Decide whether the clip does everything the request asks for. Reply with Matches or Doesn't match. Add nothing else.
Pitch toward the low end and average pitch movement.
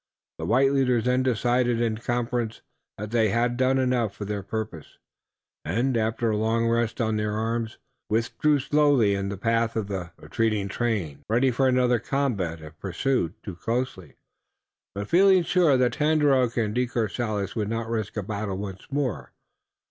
Matches